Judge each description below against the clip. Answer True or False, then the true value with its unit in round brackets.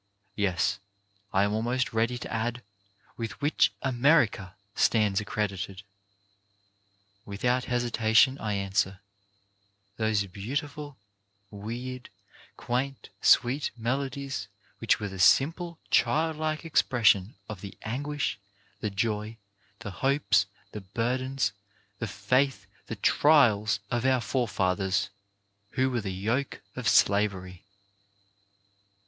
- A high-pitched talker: False (115 Hz)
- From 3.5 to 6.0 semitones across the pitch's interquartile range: True (4.5 semitones)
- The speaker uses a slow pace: True (105 wpm)